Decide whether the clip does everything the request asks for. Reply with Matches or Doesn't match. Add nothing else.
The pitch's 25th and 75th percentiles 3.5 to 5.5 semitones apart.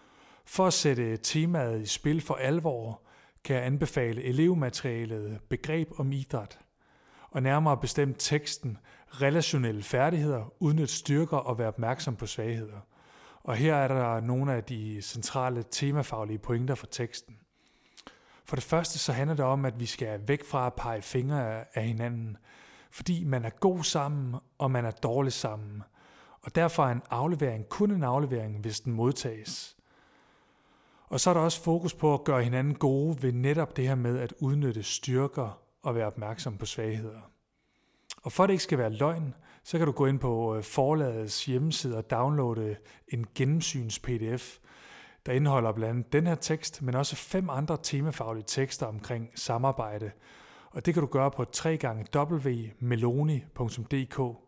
Matches